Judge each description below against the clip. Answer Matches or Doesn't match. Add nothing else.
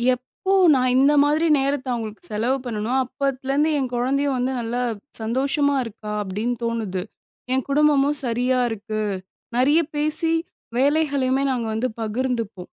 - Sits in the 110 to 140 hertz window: Doesn't match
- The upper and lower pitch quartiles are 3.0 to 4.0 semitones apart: Matches